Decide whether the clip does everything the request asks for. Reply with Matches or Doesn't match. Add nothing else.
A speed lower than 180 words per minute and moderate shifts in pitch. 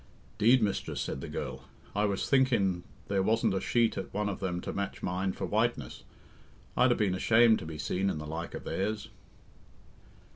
Doesn't match